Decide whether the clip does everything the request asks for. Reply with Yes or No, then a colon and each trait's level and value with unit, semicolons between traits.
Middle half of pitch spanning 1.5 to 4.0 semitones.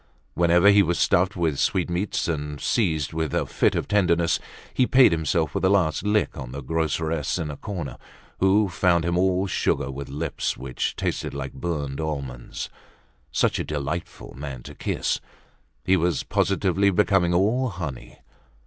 No: average, 4.4 semitones